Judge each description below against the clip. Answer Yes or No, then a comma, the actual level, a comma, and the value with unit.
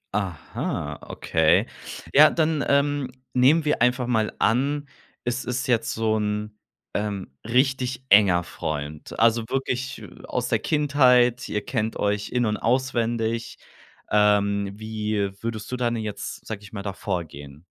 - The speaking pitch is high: No, low, 115 Hz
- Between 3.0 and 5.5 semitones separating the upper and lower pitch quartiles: Yes, average, 3.6 semitones